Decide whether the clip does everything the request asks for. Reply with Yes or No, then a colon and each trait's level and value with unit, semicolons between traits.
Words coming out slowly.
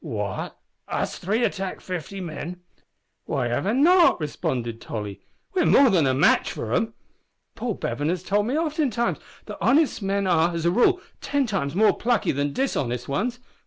No: average, 160 wpm